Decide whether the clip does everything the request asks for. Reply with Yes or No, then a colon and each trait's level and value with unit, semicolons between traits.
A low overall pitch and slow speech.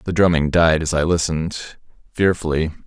Yes: very low, 80 Hz; slow, 125 wpm